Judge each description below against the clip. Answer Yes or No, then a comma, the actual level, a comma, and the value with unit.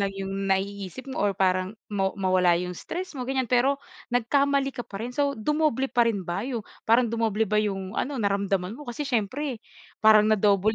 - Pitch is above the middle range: Yes, high, 215 Hz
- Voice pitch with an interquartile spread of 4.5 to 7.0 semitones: Yes, average, 4.9 semitones